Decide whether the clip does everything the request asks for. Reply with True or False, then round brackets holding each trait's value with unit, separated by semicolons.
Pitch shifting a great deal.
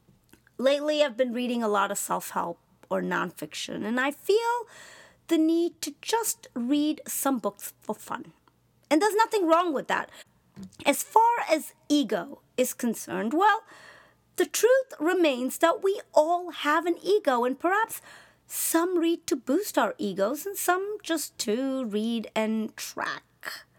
True (6.1 semitones)